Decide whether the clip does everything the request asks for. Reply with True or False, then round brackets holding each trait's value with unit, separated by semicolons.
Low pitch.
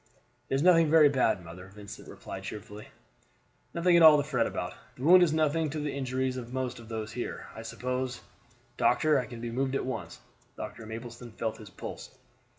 True (125 Hz)